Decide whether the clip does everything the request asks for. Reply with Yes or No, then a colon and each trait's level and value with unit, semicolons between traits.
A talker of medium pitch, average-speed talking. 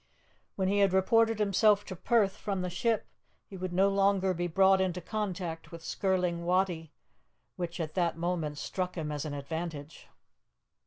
Yes: medium, 180 Hz; average, 165 wpm